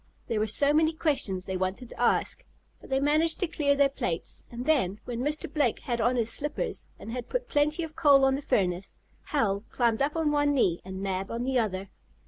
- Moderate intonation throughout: No, wide, 5.8 semitones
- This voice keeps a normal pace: No, fast, 220 wpm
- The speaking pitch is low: No, very high, 260 Hz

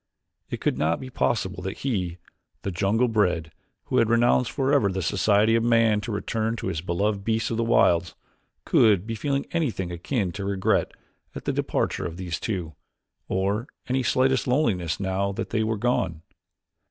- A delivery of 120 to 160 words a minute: No, average, 175 wpm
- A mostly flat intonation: No, average, 3.9 semitones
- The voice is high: No, low, 105 Hz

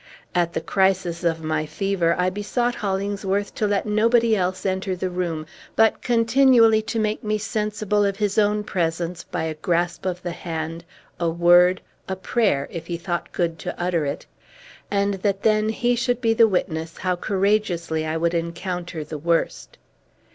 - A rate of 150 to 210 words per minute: Yes, average, 170 wpm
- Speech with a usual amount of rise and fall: Yes, average, 3.8 semitones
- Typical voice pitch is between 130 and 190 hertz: Yes, medium, 185 Hz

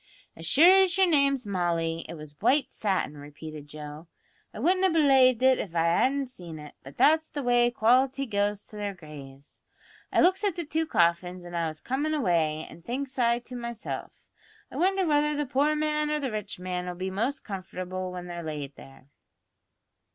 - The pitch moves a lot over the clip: Yes, wide, 8.9 semitones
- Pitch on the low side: No, high, 215 Hz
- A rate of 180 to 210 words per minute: Yes, average, 195 wpm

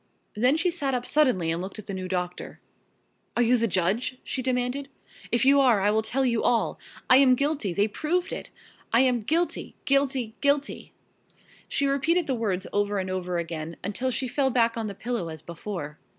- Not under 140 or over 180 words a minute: No, average, 195 wpm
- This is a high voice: Yes, high, 235 Hz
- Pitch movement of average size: No, wide, 5.8 semitones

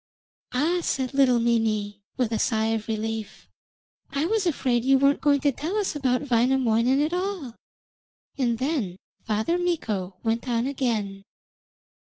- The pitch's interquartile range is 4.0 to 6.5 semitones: Yes, average, 4.3 semitones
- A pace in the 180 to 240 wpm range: No, average, 145 wpm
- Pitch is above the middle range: Yes, very high, 250 Hz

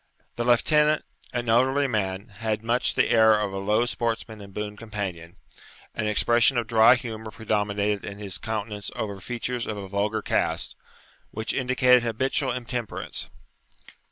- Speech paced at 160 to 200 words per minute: No, average, 150 wpm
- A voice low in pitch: Yes, low, 110 Hz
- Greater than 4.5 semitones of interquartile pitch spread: No, average, 2.7 semitones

